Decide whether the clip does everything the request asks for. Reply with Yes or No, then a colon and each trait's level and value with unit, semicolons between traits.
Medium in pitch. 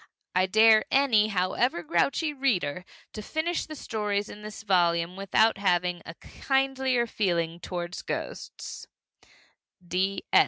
No: high, 205 Hz